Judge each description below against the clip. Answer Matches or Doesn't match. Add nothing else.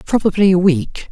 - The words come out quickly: Doesn't match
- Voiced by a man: Doesn't match